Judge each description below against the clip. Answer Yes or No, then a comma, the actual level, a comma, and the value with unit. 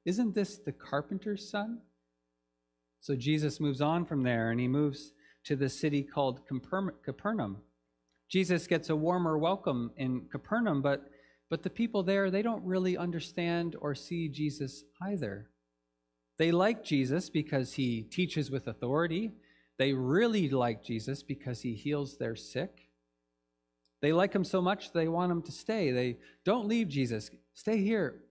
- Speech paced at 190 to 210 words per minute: No, average, 155 wpm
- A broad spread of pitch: Yes, wide, 6.9 semitones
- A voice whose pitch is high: No, medium, 145 Hz